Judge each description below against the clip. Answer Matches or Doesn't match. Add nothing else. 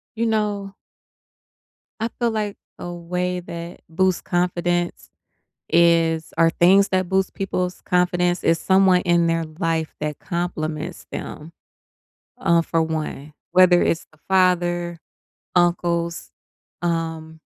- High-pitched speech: Doesn't match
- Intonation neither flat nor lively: Doesn't match